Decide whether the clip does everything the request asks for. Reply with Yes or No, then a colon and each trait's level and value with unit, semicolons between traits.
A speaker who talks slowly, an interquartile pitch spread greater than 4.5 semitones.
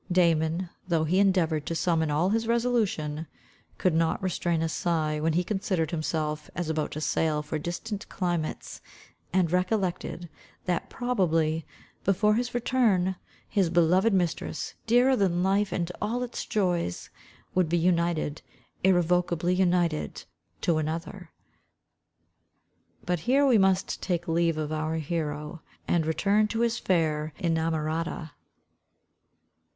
No: slow, 130 wpm; average, 3.1 semitones